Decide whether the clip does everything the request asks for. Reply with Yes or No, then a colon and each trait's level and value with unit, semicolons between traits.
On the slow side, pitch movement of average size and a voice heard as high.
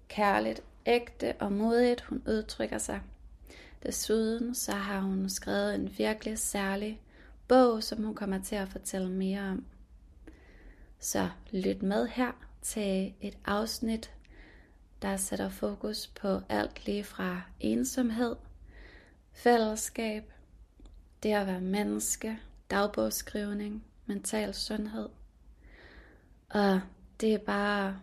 Yes: slow, 110 wpm; average, 3.1 semitones; high, 205 Hz